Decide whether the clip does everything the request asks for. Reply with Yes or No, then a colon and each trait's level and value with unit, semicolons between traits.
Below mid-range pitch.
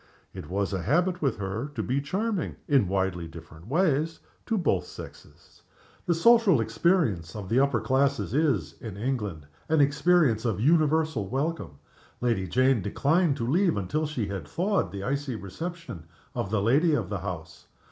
Yes: low, 130 Hz